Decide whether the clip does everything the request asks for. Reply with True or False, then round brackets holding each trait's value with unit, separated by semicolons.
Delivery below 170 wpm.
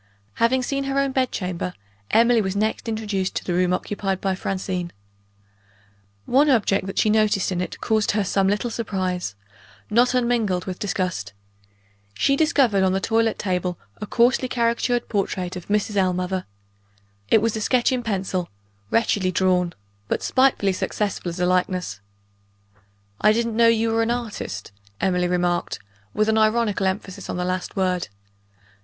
True (160 wpm)